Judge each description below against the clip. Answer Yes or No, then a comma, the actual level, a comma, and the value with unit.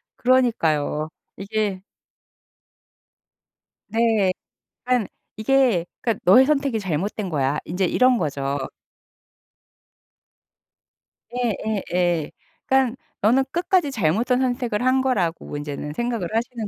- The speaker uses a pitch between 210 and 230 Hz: Yes, high, 220 Hz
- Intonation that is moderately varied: No, wide, 6.3 semitones